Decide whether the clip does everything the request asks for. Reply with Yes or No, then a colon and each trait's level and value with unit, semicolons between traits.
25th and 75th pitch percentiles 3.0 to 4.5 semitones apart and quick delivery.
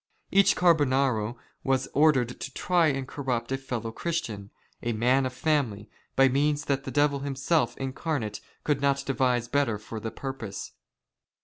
No: average, 3.3 semitones; average, 155 wpm